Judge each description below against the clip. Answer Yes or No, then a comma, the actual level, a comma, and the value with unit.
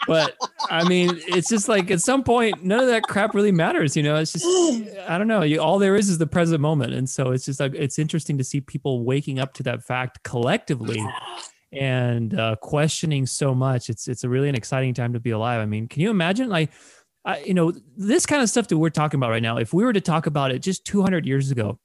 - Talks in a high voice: No, medium, 155 Hz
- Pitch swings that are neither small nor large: No, wide, 6.9 semitones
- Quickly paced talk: Yes, fast, 255 wpm